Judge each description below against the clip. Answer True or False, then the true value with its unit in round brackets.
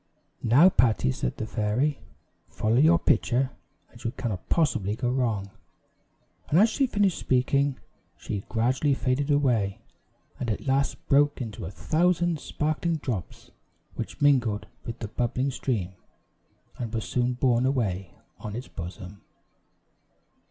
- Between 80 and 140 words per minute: True (135 wpm)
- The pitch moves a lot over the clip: False (4.8 semitones)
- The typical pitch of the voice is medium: False (125 Hz)